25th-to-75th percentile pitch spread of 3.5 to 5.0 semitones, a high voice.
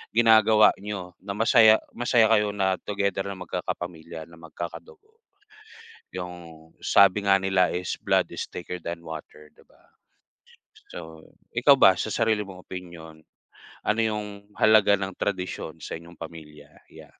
No: average, 4.0 semitones; very low, 95 Hz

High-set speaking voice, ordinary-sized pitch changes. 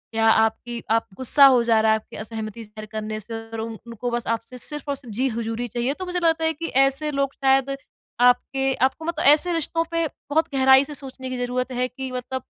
Yes: very high, 255 Hz; average, 3.5 semitones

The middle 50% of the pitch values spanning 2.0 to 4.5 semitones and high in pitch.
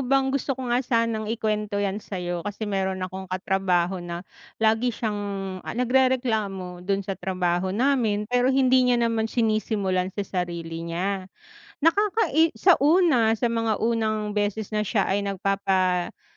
Yes: average, 4.1 semitones; high, 210 Hz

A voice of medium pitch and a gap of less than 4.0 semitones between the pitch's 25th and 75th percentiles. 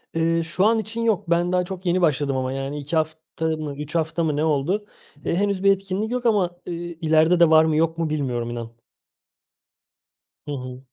Yes: medium, 165 Hz; average, 3.6 semitones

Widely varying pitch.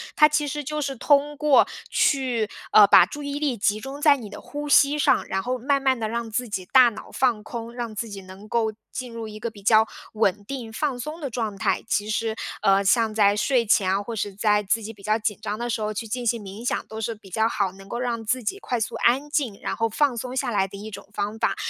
No: average, 3.8 semitones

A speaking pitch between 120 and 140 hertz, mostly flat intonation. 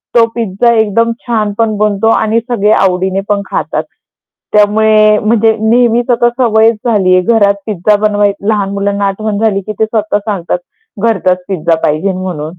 No: high, 210 Hz; narrow, 2.2 semitones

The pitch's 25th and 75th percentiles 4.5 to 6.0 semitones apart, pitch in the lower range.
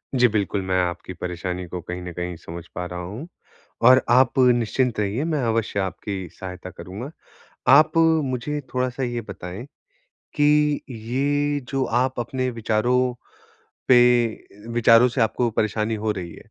Yes: average, 5.2 semitones; low, 115 Hz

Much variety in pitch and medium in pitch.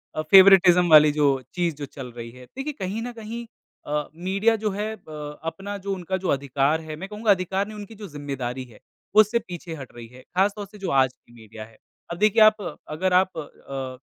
Yes: wide, 6.2 semitones; medium, 175 Hz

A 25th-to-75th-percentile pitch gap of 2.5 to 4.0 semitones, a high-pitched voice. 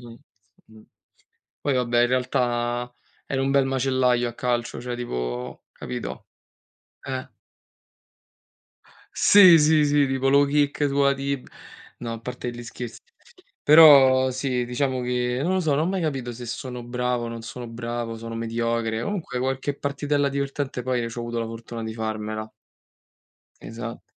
No: average, 2.8 semitones; low, 125 Hz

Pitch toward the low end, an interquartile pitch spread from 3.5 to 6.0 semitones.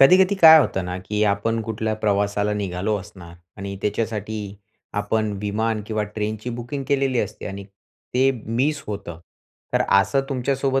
Yes: low, 110 Hz; average, 3.9 semitones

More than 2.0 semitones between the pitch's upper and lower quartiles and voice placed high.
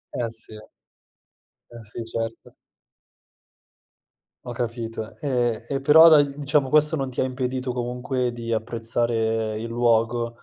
No: narrow, 2.4 semitones; low, 120 Hz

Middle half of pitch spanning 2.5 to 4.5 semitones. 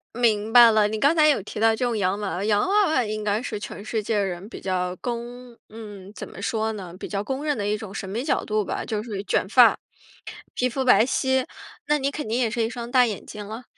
Yes: average, 3.1 semitones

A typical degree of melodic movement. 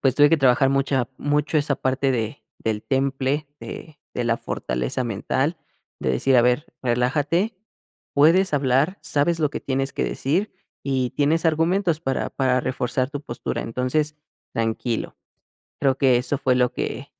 Yes: average, 3.1 semitones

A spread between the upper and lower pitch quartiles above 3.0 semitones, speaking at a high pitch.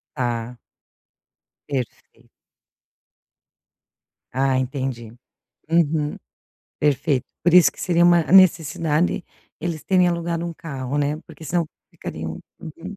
No: average, 4.5 semitones; medium, 150 Hz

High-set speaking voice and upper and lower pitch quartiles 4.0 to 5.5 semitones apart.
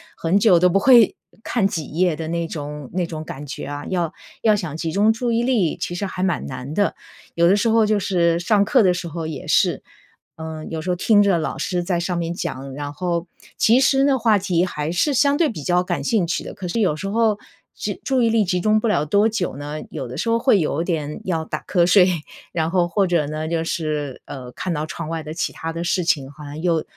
No: medium, 175 Hz; average, 4.5 semitones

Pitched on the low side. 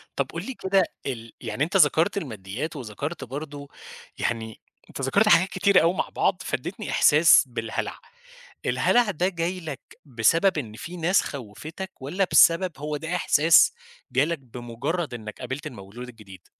No: medium, 150 Hz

